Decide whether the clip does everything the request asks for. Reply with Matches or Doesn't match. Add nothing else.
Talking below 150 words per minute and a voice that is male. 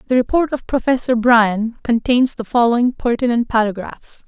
Doesn't match